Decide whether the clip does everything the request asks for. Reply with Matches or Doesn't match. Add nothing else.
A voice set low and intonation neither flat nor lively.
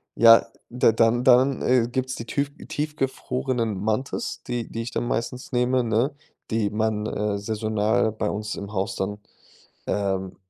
Matches